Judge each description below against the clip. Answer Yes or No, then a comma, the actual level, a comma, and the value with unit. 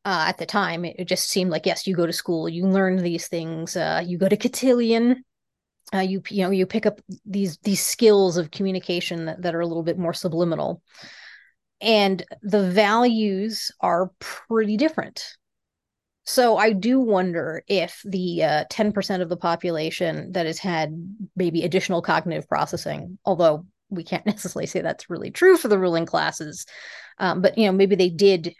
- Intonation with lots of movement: No, average, 3.1 semitones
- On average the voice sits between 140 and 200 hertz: Yes, medium, 185 Hz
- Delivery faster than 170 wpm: Yes, average, 180 wpm